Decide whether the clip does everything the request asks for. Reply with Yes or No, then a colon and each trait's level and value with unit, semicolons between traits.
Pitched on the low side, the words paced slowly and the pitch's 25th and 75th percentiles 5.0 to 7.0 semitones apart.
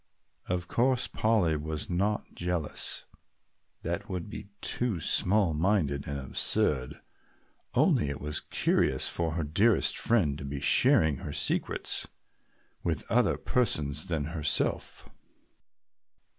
Yes: very low, 85 Hz; slow, 115 wpm; wide, 5.4 semitones